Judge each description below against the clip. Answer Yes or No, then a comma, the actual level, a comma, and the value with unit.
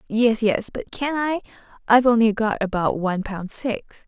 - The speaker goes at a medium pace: Yes, average, 175 wpm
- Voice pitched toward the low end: No, high, 225 Hz